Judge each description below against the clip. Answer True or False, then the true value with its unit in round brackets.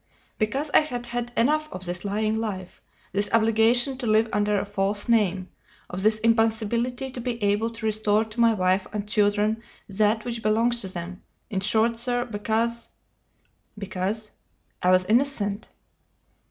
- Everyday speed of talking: True (160 wpm)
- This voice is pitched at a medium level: False (220 Hz)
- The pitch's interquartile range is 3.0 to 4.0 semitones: False (2.5 semitones)